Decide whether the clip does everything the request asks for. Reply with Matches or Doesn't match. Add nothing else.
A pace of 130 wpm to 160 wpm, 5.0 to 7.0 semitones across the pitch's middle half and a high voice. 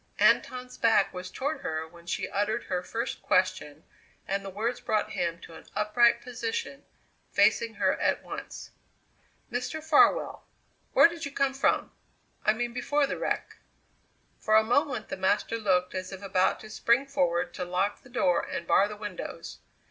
Doesn't match